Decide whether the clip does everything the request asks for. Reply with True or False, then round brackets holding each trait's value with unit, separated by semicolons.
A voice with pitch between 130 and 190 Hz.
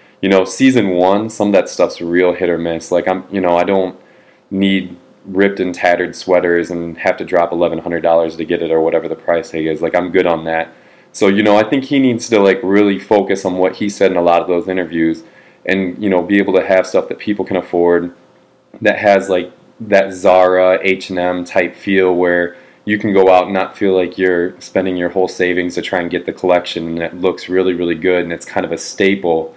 False (90 Hz)